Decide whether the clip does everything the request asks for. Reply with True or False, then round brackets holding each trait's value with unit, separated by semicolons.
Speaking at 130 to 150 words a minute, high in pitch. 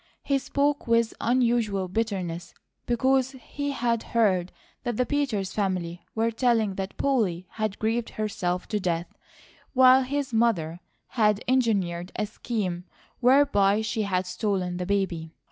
True (135 wpm; 215 Hz)